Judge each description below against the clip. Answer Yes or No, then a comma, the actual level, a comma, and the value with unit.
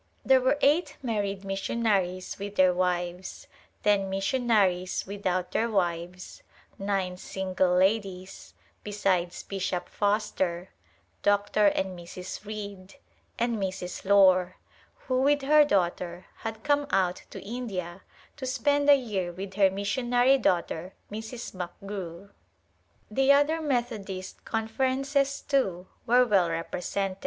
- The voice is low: No, high, 200 Hz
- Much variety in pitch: No, average, 4.4 semitones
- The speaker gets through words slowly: Yes, slow, 115 wpm